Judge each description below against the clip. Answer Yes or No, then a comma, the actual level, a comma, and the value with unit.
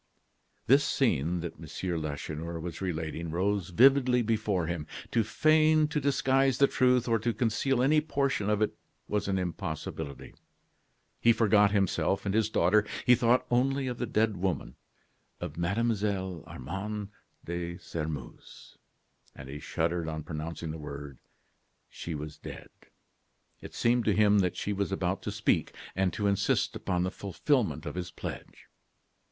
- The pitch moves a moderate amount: No, wide, 5.8 semitones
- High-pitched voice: No, low, 100 Hz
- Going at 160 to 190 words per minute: No, average, 150 wpm